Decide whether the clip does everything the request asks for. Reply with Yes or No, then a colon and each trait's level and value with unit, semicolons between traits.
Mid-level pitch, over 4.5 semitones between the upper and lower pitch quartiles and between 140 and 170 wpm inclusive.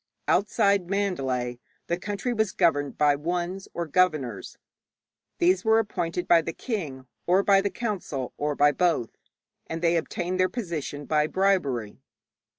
Yes: medium, 175 Hz; average, 4.9 semitones; average, 145 wpm